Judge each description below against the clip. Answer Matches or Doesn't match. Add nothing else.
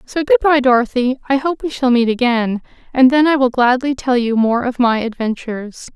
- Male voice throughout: Doesn't match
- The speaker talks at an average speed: Doesn't match